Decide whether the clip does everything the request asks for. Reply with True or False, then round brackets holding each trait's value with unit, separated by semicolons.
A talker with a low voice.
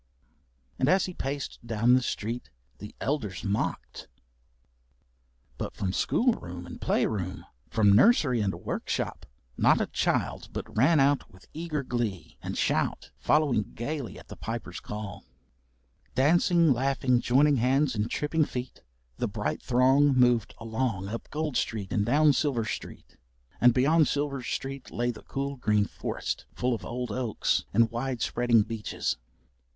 True (125 Hz)